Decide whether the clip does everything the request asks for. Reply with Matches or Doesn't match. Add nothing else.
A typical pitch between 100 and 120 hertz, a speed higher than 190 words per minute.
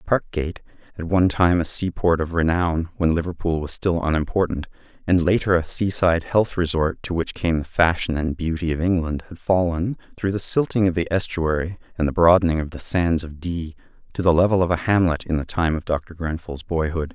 Doesn't match